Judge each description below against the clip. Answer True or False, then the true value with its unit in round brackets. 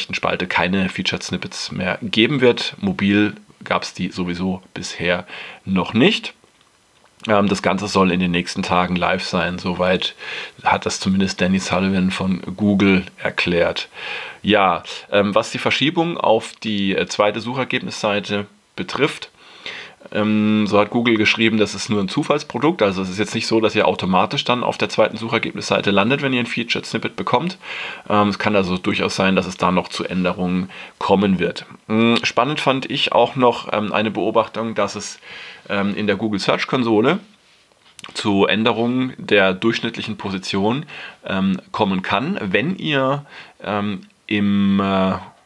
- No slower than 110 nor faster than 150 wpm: True (145 wpm)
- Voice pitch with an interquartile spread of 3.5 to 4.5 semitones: False (2.6 semitones)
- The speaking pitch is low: True (100 Hz)